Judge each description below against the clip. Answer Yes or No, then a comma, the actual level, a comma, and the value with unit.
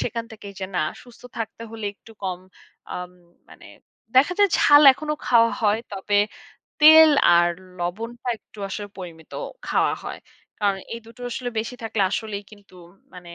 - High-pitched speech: Yes, high, 220 Hz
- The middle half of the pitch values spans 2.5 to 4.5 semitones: Yes, average, 3.6 semitones